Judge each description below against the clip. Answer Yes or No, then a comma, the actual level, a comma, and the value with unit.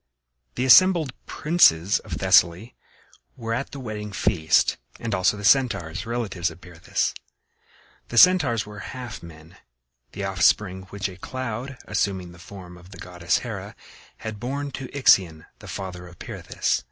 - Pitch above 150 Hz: No, low, 100 Hz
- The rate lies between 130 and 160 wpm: Yes, average, 150 wpm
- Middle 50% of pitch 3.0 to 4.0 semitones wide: No, wide, 5.6 semitones